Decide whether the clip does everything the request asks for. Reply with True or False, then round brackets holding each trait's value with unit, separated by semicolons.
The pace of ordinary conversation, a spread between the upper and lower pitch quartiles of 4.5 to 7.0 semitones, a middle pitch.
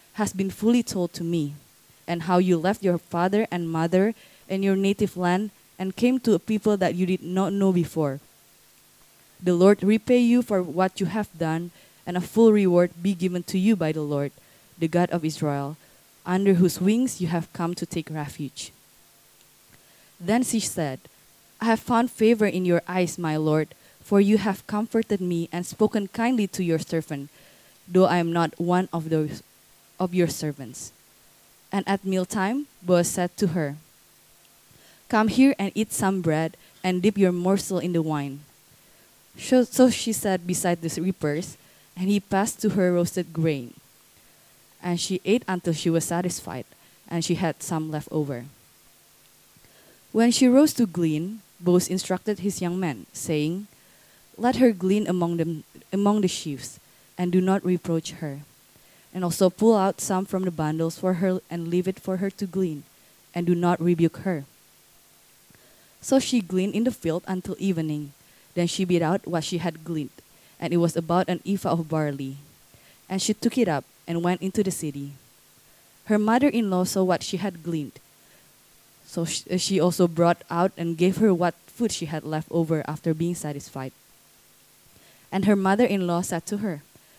False (175 wpm; 3.1 semitones; 180 Hz)